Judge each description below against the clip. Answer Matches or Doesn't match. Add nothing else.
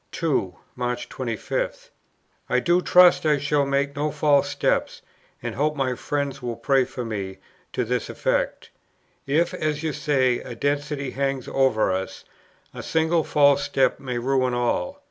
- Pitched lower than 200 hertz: Matches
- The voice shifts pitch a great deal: Doesn't match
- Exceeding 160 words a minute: Doesn't match